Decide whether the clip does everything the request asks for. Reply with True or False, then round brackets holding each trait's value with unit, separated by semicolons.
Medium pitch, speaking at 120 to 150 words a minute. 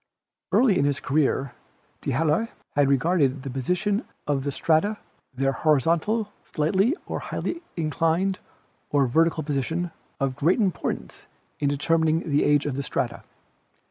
True (155 Hz; 135 wpm)